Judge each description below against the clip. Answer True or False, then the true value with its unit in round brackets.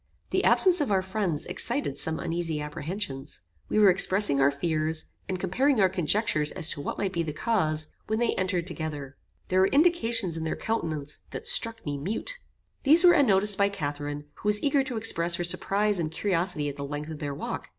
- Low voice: False (185 Hz)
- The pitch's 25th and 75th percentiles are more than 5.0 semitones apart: True (5.6 semitones)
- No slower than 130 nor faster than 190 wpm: False (200 wpm)